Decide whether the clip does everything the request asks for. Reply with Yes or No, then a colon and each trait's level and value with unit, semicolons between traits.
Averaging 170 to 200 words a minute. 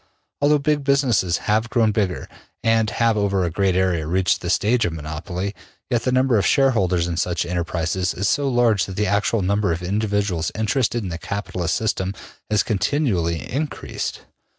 Yes: average, 175 wpm